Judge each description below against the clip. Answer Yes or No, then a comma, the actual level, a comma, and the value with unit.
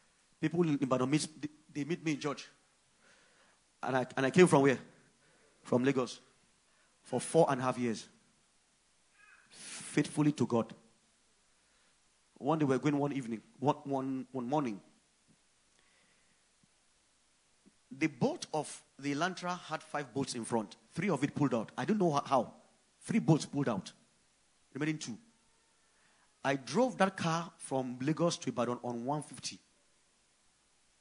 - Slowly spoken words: No, average, 145 wpm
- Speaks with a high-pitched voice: No, medium, 145 Hz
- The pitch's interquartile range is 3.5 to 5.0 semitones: Yes, average, 4.1 semitones